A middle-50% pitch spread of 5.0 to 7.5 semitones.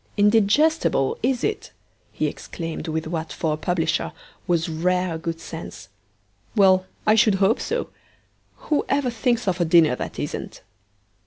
Yes: wide, 5.6 semitones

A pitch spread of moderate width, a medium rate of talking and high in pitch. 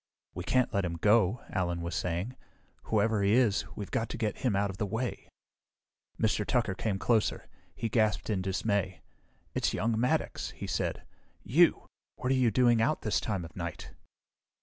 No: average, 3.5 semitones; average, 175 wpm; low, 105 Hz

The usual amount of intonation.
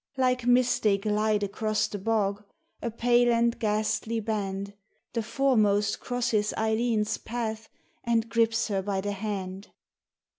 No: narrow, 2.2 semitones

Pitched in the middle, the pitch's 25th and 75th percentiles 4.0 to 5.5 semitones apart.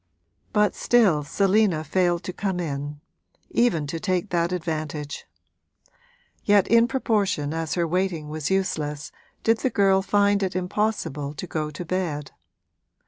Yes: medium, 180 Hz; average, 4.6 semitones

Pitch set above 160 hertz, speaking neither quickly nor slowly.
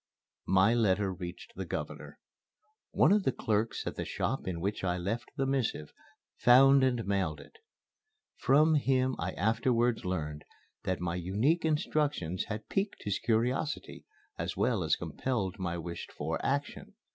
No: low, 110 Hz; average, 150 wpm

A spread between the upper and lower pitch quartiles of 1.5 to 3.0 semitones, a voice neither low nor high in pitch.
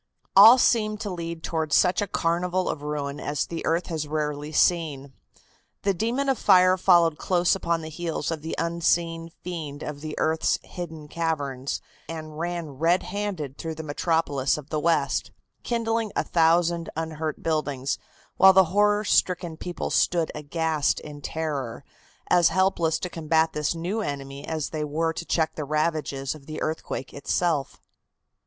Yes: average, 2.7 semitones; medium, 165 Hz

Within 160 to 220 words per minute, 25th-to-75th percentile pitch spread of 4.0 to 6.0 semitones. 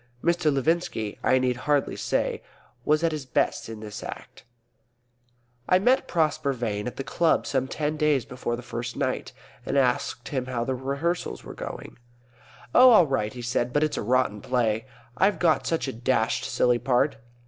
Yes: average, 175 wpm; average, 4.3 semitones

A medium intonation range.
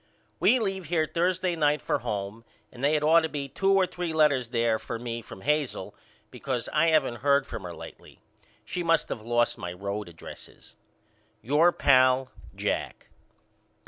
No: wide, 5.9 semitones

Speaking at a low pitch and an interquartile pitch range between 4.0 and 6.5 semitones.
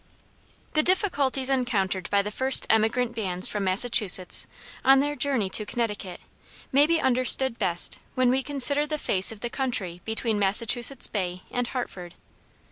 No: high, 235 Hz; average, 5.2 semitones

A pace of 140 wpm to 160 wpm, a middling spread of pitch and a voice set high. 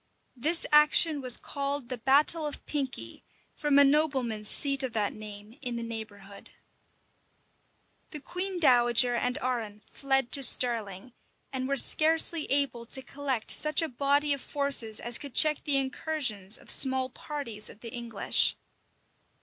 Yes: average, 150 wpm; average, 3.7 semitones; very high, 265 Hz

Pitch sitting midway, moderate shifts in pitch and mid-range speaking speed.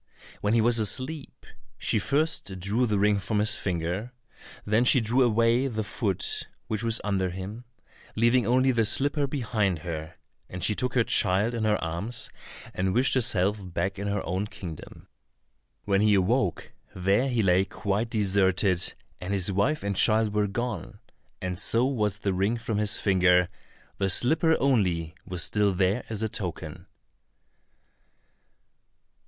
No: low, 105 Hz; average, 3.8 semitones; average, 155 wpm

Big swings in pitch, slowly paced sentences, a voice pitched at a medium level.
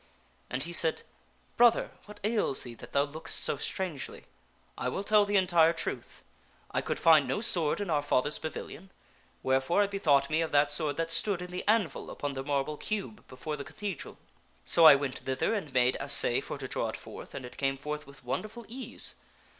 No: wide, 5.9 semitones; average, 200 wpm; medium, 155 Hz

